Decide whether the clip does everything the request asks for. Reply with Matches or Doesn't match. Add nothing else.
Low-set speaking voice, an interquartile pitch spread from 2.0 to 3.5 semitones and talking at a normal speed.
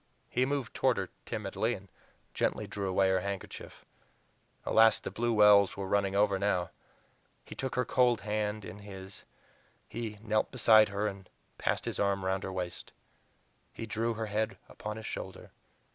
Matches